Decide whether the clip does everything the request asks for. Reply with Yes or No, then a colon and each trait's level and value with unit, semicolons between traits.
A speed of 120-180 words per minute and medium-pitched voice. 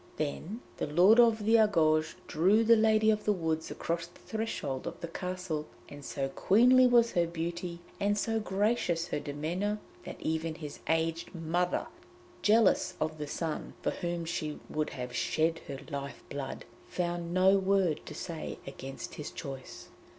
Yes: average, 165 wpm; medium, 170 Hz